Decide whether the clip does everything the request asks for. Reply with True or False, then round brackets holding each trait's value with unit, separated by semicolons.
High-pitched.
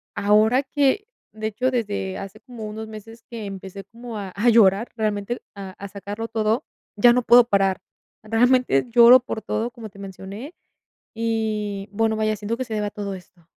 True (215 Hz)